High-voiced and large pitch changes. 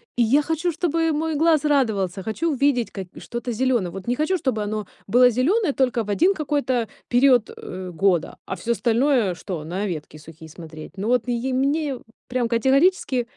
Yes: high, 245 Hz; wide, 6.2 semitones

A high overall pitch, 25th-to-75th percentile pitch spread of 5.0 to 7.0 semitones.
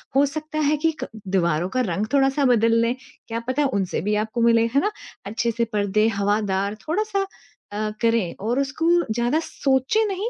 Yes: high, 235 Hz; average, 5.3 semitones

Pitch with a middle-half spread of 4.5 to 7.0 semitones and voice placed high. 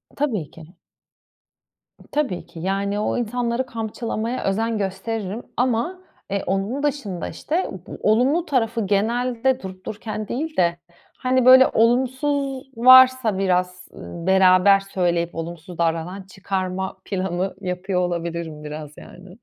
Yes: average, 5.3 semitones; high, 200 Hz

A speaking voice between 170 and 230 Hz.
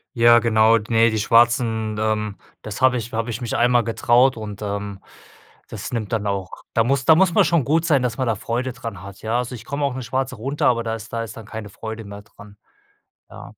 No: low, 115 Hz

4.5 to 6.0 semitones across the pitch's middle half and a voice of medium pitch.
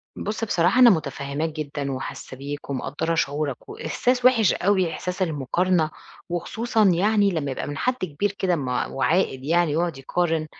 Yes: average, 4.8 semitones; medium, 165 Hz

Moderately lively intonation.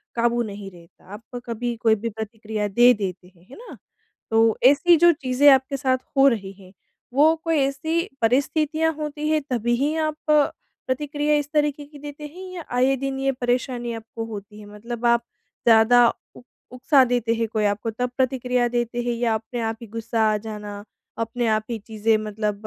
Yes: average, 4.0 semitones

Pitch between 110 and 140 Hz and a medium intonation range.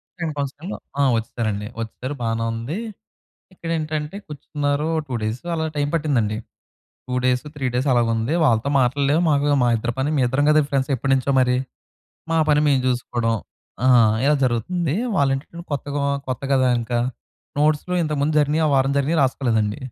Yes: low, 135 Hz; average, 3.7 semitones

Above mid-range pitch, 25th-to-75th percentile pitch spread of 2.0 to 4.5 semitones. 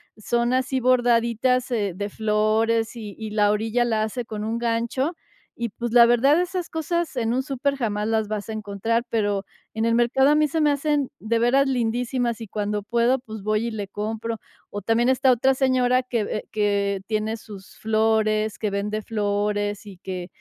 Yes: high, 225 Hz; average, 2.8 semitones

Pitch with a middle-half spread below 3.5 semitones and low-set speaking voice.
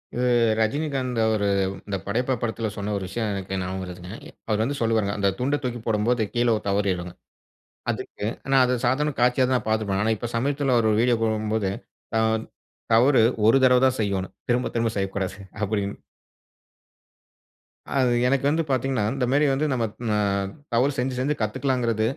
No: average, 3.8 semitones; low, 115 Hz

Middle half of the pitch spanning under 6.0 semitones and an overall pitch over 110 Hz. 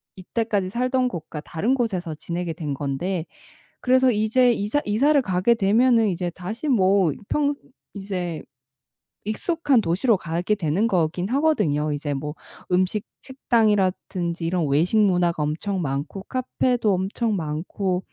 Yes: wide, 5.4 semitones; high, 190 Hz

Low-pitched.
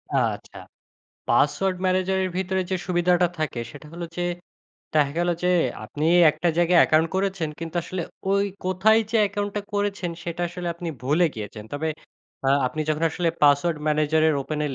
No: medium, 175 Hz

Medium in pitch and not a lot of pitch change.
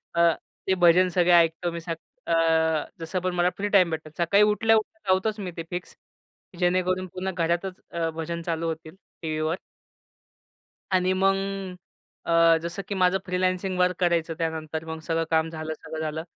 Yes: medium, 175 Hz; narrow, 2.2 semitones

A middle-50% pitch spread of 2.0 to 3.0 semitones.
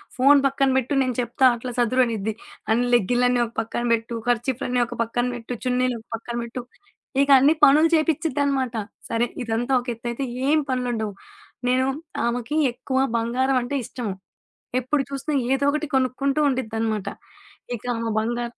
Yes: narrow, 2.5 semitones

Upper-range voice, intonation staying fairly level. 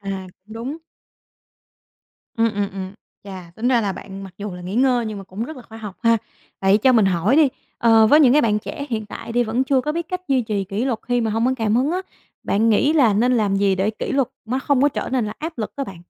No: high, 225 Hz; average, 4.4 semitones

